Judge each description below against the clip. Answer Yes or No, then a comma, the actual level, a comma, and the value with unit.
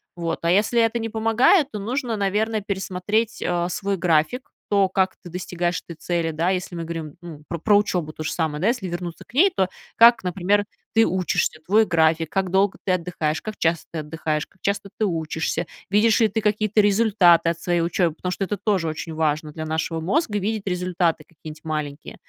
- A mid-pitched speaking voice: Yes, medium, 180 Hz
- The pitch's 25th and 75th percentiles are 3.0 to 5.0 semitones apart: Yes, average, 4.1 semitones